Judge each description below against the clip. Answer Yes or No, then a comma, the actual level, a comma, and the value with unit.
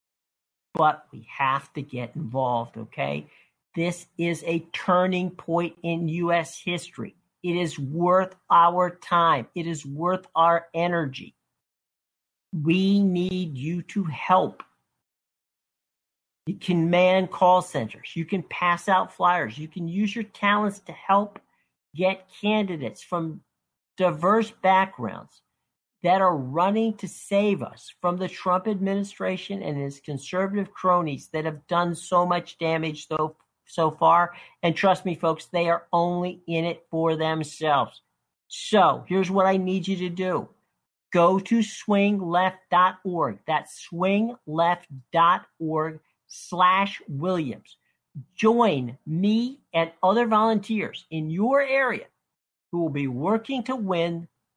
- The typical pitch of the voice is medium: Yes, medium, 175 Hz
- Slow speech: Yes, slow, 125 wpm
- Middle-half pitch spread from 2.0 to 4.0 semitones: Yes, average, 2.9 semitones